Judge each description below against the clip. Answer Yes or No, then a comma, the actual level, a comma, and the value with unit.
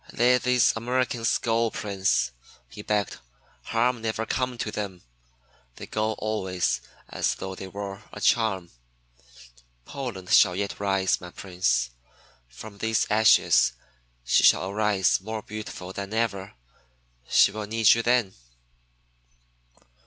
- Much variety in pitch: No, average, 3.0 semitones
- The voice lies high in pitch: No, low, 105 Hz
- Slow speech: Yes, slow, 125 wpm